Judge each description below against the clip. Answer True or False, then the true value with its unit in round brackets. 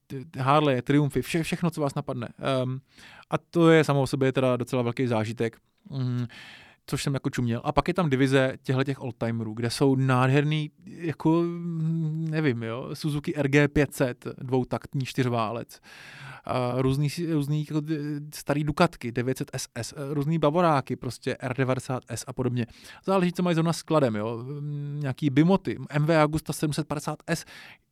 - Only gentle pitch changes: False (3.2 semitones)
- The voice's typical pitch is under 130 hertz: False (140 Hz)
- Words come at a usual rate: True (140 wpm)